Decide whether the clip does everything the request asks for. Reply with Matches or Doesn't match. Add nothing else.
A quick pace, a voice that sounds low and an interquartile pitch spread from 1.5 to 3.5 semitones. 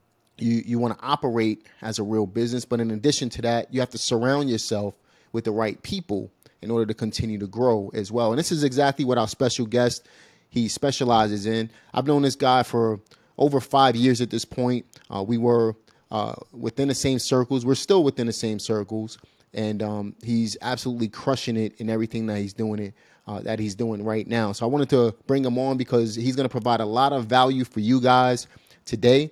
Matches